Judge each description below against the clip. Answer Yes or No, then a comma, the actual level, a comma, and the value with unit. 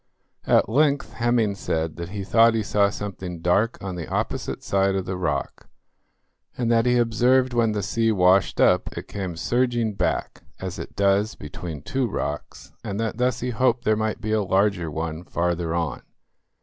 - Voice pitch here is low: Yes, low, 100 Hz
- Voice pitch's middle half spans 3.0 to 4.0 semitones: No, average, 4.6 semitones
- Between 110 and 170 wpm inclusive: No, average, 180 wpm